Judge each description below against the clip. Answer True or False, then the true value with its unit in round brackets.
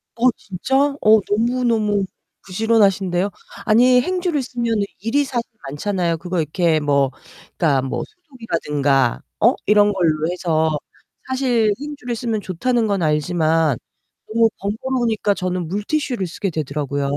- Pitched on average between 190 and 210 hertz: True (200 Hz)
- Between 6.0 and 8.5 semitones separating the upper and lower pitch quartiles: True (6.4 semitones)